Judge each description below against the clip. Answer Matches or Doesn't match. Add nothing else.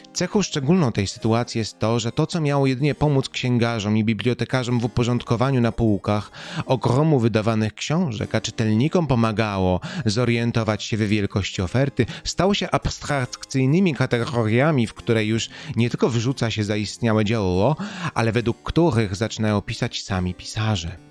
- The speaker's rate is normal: Matches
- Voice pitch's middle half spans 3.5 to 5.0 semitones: Matches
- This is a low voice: Matches